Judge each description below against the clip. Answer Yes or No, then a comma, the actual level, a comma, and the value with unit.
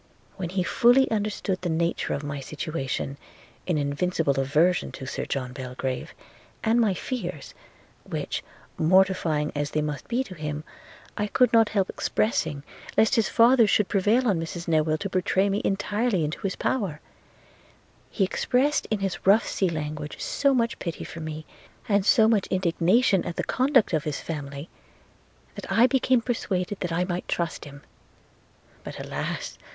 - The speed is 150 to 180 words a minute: Yes, average, 160 wpm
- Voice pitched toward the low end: No, medium, 185 Hz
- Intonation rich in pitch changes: Yes, wide, 5.9 semitones